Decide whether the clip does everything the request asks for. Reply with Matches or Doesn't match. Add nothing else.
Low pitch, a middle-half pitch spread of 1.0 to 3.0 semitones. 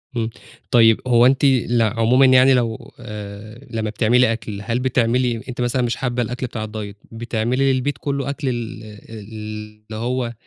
Matches